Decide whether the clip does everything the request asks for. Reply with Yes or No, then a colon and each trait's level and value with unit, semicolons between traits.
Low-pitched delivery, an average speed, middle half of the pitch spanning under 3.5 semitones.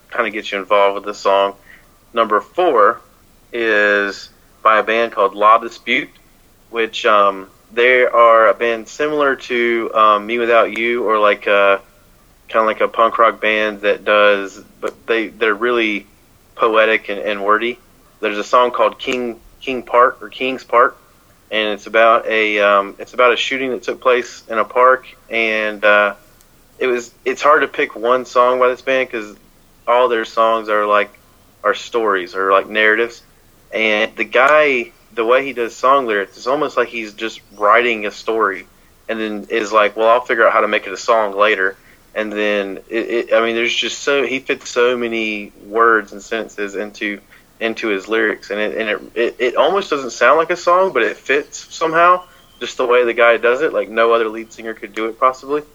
Yes: low, 115 Hz; average, 195 wpm; average, 2.7 semitones